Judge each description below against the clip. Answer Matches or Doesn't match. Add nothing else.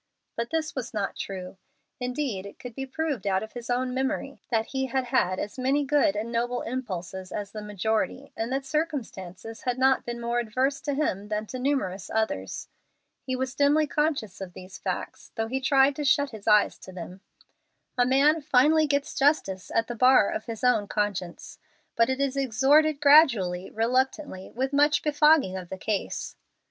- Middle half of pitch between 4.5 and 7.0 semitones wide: Matches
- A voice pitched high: Matches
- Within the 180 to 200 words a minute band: Matches